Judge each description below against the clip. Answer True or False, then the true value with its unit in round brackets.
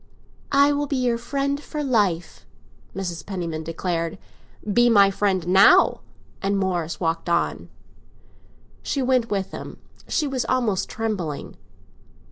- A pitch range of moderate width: False (6.5 semitones)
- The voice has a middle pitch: False (200 Hz)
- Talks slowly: True (125 wpm)